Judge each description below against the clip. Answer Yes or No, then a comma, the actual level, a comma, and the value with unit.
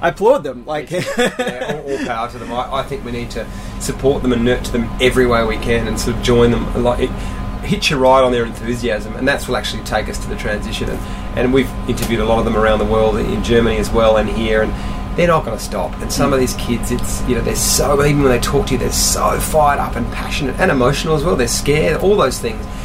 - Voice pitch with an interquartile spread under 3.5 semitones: Yes, average, 3.0 semitones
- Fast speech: Yes, fast, 260 wpm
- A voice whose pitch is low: Yes, low, 120 Hz